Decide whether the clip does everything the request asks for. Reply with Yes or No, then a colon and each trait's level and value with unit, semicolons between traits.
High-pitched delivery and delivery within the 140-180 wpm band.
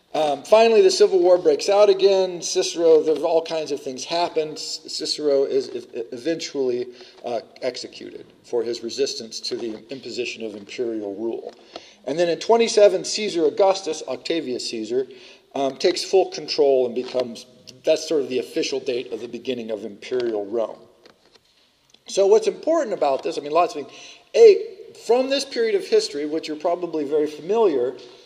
Yes: high, 210 Hz; average, 160 wpm